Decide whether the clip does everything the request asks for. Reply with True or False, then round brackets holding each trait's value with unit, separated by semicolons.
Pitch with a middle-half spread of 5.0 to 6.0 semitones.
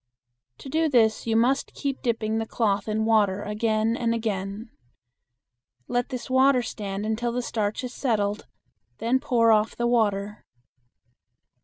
False (2.4 semitones)